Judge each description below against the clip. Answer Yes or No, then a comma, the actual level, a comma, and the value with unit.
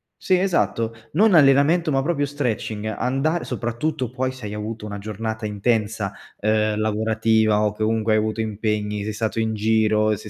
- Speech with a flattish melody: No, average, 3.3 semitones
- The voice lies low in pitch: Yes, low, 110 Hz